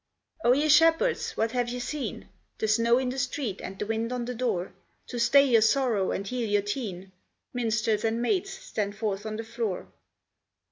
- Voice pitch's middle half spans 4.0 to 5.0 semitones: No, average, 2.9 semitones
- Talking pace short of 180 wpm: No, average, 190 wpm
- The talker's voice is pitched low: No, high, 230 Hz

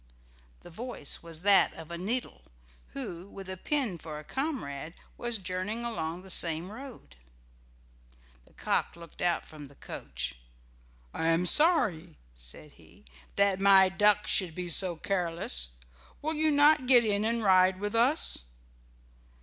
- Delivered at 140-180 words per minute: Yes, average, 150 wpm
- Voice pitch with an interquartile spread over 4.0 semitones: Yes, wide, 5.6 semitones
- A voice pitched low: No, medium, 185 Hz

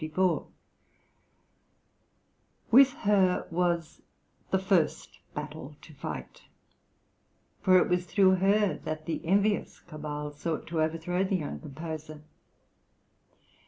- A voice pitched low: No, medium, 170 Hz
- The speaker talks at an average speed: No, slow, 100 wpm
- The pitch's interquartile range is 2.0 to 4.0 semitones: Yes, average, 3.5 semitones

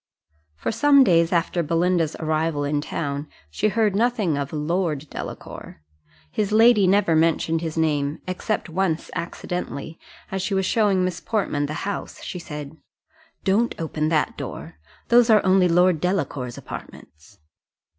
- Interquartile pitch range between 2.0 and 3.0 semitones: No, average, 4.1 semitones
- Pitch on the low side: No, medium, 170 Hz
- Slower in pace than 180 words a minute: Yes, average, 145 wpm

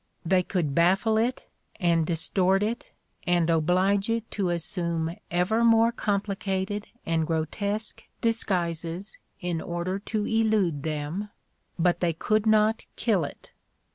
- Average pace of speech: No, slow, 130 wpm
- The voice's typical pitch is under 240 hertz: Yes, medium, 185 Hz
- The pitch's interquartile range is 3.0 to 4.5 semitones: Yes, average, 4.1 semitones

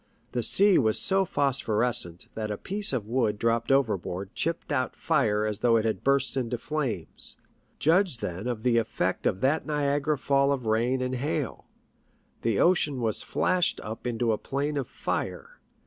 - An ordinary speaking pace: Yes, average, 175 wpm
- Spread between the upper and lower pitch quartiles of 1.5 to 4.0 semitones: No, average, 4.5 semitones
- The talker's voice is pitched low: Yes, low, 125 Hz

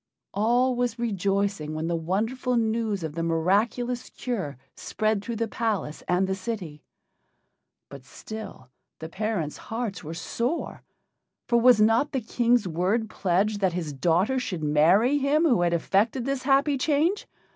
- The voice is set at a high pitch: Yes, high, 215 Hz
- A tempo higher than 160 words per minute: No, average, 150 wpm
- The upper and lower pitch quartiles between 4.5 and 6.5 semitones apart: Yes, wide, 5.6 semitones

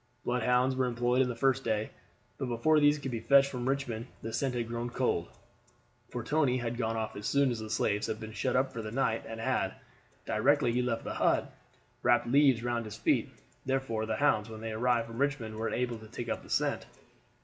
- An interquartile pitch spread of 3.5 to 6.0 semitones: No, average, 2.7 semitones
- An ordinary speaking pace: No, fast, 215 wpm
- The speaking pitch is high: No, low, 120 Hz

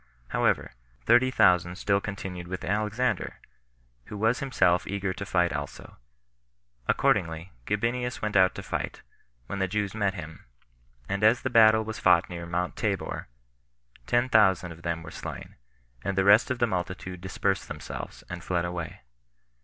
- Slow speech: No, average, 155 wpm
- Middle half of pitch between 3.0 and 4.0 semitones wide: Yes, average, 3.6 semitones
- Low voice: Yes, very low, 95 Hz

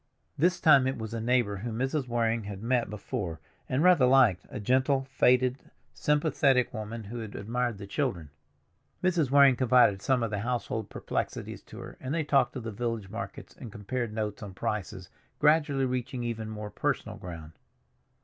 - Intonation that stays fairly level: No, average, 3.8 semitones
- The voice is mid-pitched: No, low, 120 Hz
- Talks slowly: No, average, 175 wpm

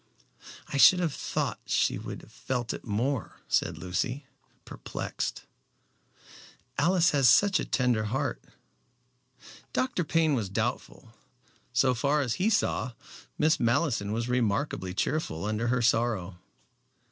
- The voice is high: No, low, 125 Hz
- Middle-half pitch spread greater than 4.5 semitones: Yes, average, 5.1 semitones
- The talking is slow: Yes, slow, 125 wpm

